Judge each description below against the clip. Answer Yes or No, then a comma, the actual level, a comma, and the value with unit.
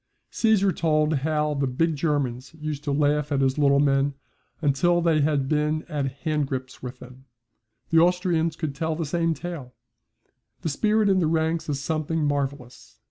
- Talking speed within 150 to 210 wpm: Yes, average, 165 wpm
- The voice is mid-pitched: Yes, medium, 150 Hz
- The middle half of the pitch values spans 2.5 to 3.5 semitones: Yes, average, 2.8 semitones